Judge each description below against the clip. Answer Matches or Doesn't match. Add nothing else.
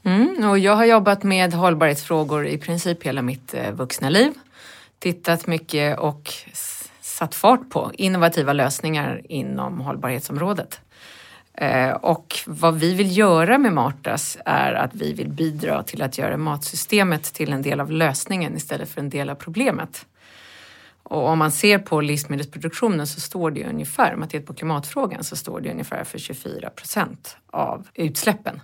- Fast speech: Doesn't match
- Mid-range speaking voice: Matches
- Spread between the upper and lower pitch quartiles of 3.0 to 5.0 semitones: Matches